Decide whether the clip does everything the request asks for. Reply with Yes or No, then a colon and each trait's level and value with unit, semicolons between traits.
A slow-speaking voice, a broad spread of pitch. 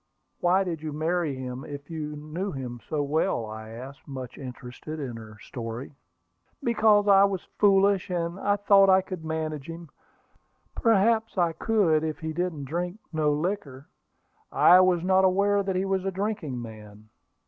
No: average, 160 wpm; wide, 5.7 semitones